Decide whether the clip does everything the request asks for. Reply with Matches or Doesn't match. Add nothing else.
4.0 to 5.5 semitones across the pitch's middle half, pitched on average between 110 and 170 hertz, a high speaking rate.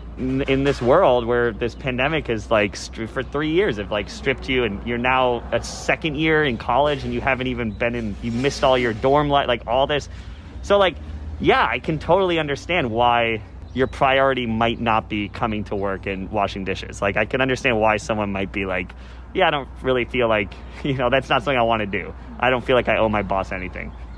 Matches